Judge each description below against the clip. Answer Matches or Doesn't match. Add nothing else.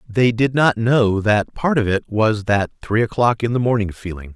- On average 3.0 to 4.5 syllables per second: Doesn't match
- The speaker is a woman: Doesn't match